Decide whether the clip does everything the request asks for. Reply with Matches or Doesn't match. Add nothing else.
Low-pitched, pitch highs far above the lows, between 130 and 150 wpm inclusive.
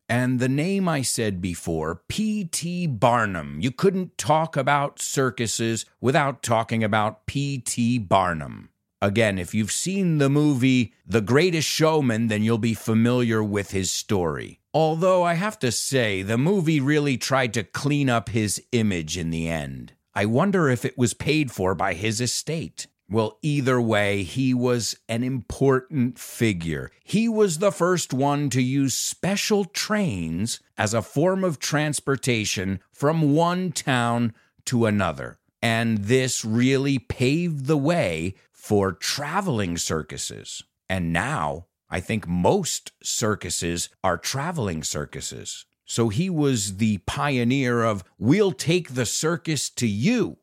Matches